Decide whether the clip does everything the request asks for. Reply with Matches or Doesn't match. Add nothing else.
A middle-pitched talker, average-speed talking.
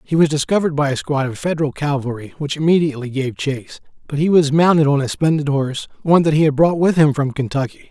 Doesn't match